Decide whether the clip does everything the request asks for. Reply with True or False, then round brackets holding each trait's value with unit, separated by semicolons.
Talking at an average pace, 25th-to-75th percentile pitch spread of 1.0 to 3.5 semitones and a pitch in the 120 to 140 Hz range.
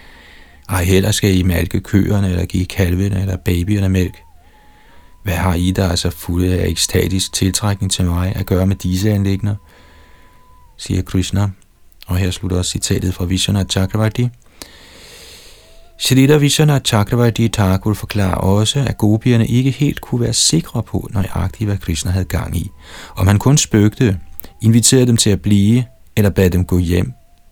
False (160 wpm; 2.9 semitones; 95 Hz)